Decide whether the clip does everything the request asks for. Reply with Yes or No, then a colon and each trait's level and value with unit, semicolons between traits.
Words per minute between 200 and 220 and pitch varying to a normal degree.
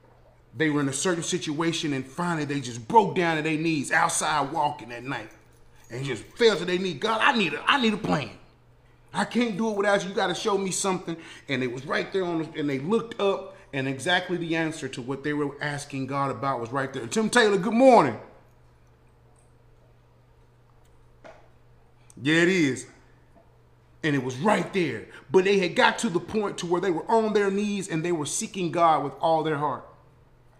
No: fast, 205 wpm; wide, 6.1 semitones